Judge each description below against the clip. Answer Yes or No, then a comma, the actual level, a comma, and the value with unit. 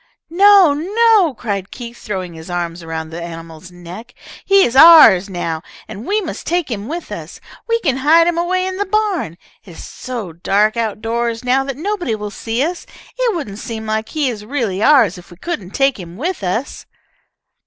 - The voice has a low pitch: No, high, 235 Hz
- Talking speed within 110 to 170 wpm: No, average, 195 wpm